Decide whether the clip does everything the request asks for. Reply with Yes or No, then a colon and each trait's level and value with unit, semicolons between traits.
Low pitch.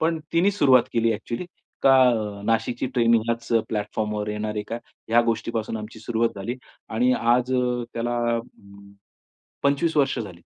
Yes: low, 115 Hz